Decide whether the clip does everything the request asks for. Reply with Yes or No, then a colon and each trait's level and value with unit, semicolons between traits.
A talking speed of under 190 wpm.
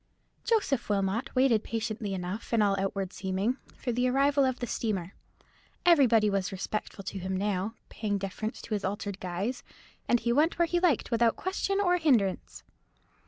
Yes: average, 165 wpm